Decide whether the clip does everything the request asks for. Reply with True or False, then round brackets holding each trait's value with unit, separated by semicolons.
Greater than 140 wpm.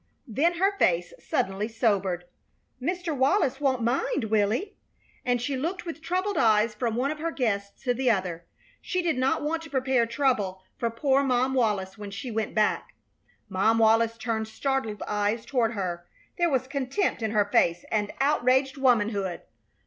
True (170 wpm)